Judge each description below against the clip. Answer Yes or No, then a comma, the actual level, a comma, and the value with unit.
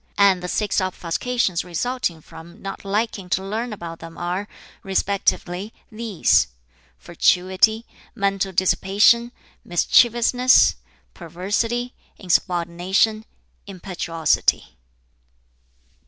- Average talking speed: No, slow, 80 wpm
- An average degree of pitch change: Yes, average, 3.7 semitones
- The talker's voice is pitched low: No, high, 195 Hz